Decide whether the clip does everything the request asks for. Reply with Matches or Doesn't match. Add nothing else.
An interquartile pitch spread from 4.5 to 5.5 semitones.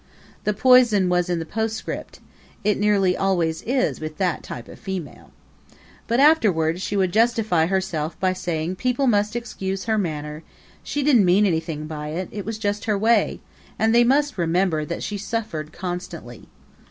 Matches